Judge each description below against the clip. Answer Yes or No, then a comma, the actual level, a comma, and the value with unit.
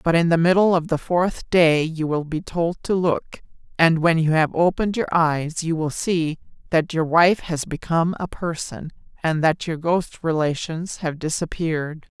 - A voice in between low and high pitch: Yes, medium, 165 Hz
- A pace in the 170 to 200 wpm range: Yes, average, 185 wpm